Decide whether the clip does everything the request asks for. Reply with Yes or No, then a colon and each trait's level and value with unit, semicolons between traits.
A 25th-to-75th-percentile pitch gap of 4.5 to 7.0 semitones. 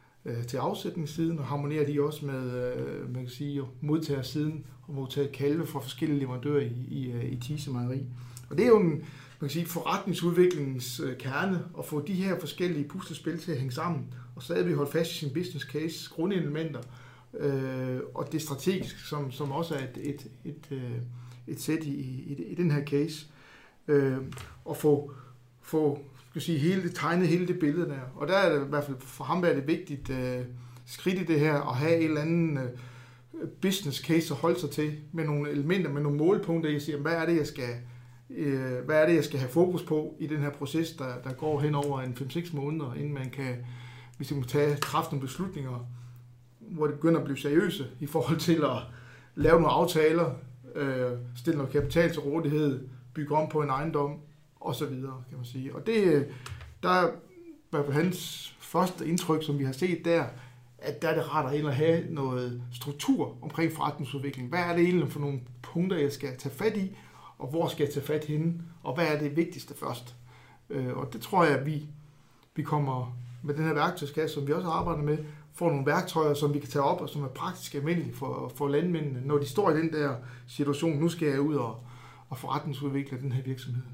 No: average, 3.5 semitones